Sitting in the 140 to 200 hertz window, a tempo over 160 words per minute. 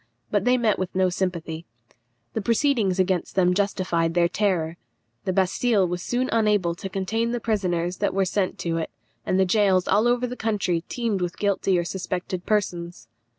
Yes: high, 190 Hz; average, 180 wpm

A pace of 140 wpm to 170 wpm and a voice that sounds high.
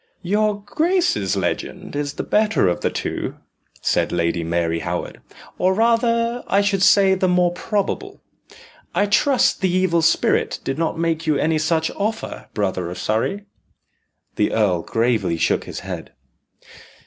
No: average, 150 wpm; medium, 170 Hz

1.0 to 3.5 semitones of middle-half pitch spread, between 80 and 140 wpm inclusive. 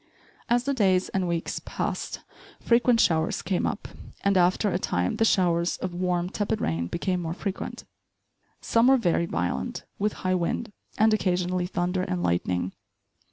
No: average, 3.2 semitones; average, 160 wpm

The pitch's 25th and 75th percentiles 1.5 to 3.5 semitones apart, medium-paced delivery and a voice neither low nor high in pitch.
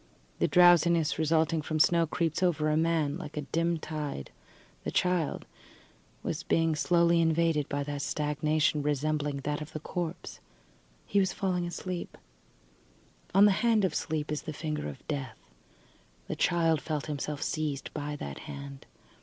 Yes: narrow, 2.4 semitones; average, 155 wpm; medium, 155 Hz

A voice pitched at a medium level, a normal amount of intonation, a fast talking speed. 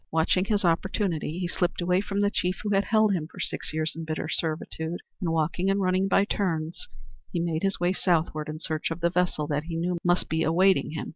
Yes: medium, 175 Hz; average, 3.0 semitones; fast, 225 wpm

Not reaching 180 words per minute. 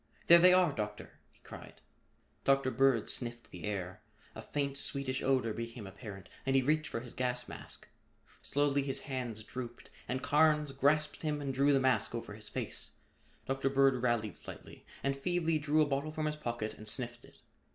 No: average, 185 wpm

